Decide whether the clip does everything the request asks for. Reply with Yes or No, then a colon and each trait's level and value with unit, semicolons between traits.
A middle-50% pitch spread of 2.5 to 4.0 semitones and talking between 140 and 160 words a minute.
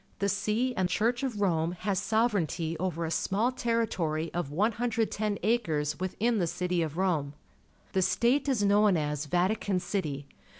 No: average, 4.9 semitones; average, 155 wpm